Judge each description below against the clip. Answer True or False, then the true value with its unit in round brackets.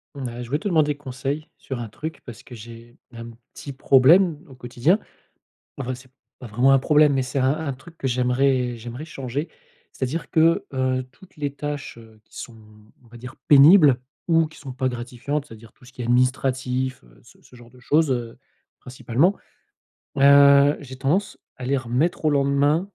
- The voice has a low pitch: True (130 Hz)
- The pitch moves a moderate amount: True (3.0 semitones)